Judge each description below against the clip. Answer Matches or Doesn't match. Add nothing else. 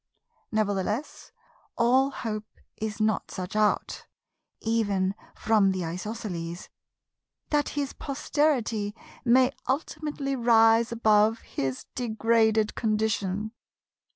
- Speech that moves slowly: Matches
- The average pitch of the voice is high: Matches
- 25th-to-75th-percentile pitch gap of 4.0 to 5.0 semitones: Doesn't match